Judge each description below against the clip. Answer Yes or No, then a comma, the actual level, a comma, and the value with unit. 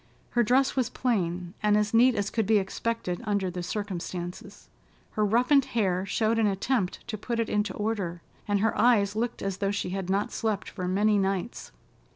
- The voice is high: Yes, high, 210 Hz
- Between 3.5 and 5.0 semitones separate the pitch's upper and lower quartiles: No, average, 3.0 semitones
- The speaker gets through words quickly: No, average, 190 wpm